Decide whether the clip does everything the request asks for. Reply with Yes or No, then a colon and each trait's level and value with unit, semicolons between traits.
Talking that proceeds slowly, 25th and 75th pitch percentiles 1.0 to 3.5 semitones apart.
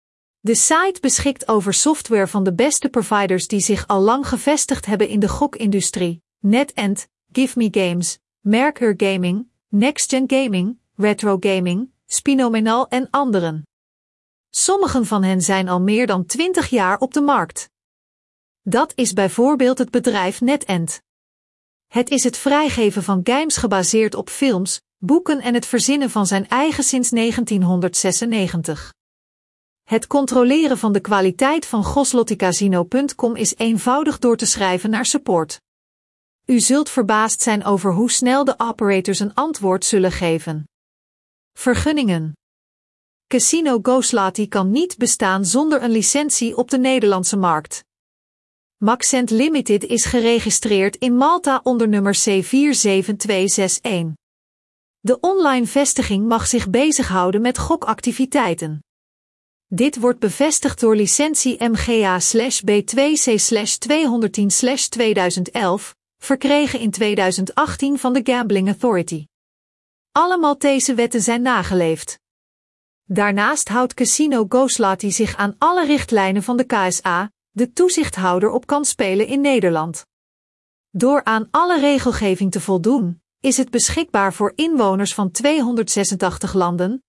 No: slow, 120 wpm; average, 5.1 semitones